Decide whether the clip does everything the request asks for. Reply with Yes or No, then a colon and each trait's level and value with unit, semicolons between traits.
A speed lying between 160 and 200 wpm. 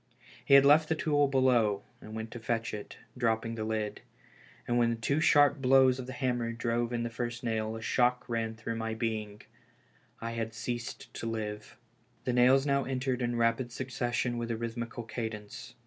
Yes: average, 190 wpm